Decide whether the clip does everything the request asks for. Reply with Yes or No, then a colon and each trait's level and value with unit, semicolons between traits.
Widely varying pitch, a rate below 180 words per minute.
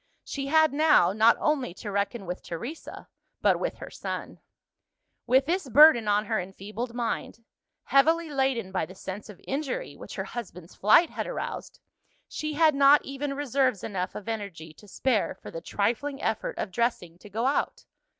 Yes: wide, 6.0 semitones; average, 170 wpm